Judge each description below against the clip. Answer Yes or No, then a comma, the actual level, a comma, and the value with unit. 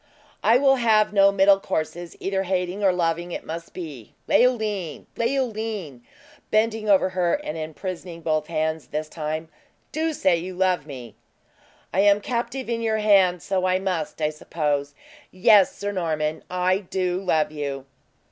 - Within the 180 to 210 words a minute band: No, average, 155 wpm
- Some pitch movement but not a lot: Yes, average, 4.6 semitones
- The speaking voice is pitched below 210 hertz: Yes, medium, 185 Hz